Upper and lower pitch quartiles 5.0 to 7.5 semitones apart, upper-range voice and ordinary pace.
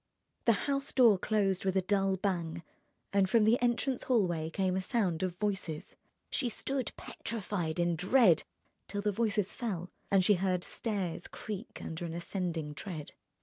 No: average, 3.8 semitones; high, 195 Hz; average, 160 wpm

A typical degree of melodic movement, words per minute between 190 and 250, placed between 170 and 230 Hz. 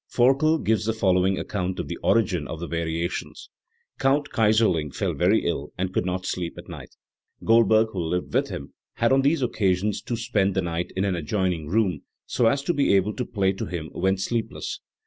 No: average, 4.2 semitones; average, 200 wpm; very low, 95 Hz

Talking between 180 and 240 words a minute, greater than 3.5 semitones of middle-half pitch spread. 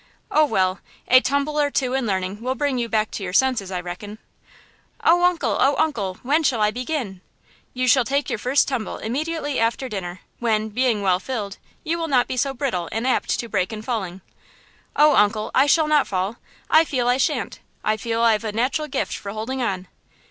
Yes: fast, 205 wpm; average, 4.9 semitones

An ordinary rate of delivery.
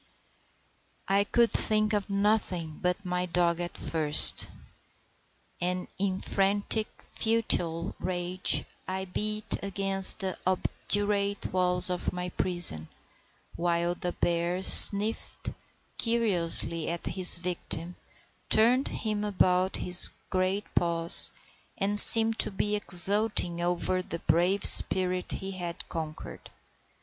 No: slow, 115 wpm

